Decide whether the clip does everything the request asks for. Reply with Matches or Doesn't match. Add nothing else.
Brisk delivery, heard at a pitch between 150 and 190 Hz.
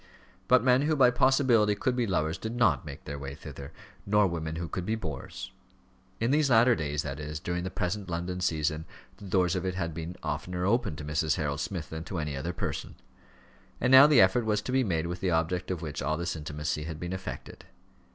Doesn't match